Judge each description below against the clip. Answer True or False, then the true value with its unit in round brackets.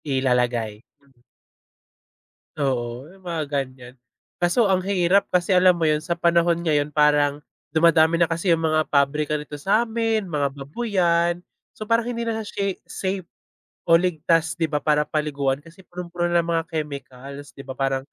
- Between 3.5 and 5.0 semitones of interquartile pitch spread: True (3.9 semitones)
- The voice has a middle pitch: True (160 Hz)